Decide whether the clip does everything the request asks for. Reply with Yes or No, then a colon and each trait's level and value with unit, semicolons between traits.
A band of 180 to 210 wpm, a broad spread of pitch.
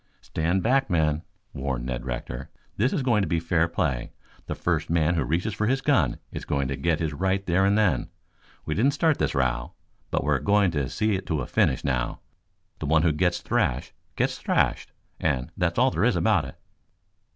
Yes: fast, 205 wpm; wide, 6.1 semitones